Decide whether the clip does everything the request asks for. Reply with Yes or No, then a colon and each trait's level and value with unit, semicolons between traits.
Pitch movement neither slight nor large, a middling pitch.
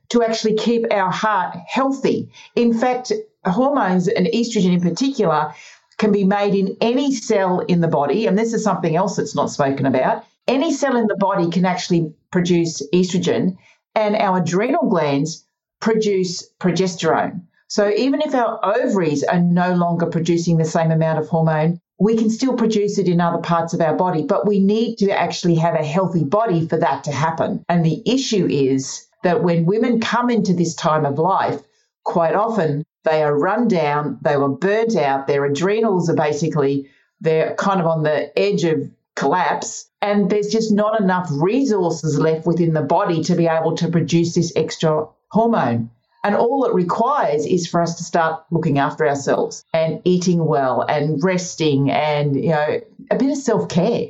Yes: average, 5.0 semitones; medium, 180 Hz